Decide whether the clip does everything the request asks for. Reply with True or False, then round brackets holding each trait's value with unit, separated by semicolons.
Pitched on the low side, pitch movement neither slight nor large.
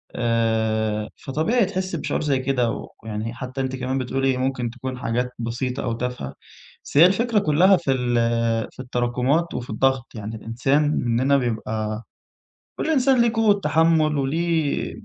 True (130 Hz; 4.9 semitones)